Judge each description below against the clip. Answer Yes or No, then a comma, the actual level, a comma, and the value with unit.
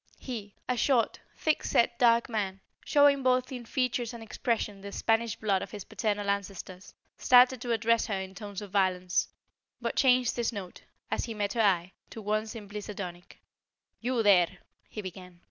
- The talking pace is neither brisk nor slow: Yes, average, 175 wpm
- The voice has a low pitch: No, high, 215 Hz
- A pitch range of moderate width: Yes, average, 3.4 semitones